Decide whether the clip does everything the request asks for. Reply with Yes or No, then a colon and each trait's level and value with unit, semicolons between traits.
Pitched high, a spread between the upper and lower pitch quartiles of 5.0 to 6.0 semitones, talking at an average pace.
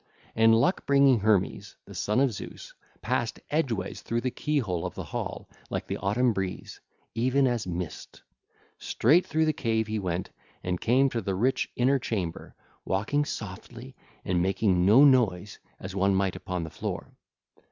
No: low, 110 Hz; wide, 5.4 semitones; average, 165 wpm